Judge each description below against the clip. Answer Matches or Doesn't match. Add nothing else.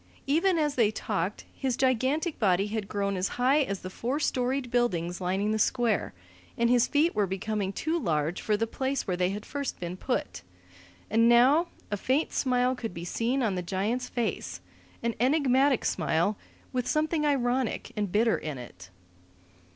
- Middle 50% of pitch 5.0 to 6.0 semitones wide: Matches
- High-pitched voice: Matches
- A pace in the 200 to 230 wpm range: Doesn't match